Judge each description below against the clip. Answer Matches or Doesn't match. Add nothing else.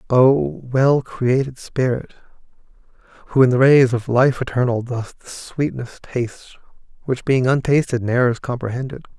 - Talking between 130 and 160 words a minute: Matches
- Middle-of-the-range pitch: Doesn't match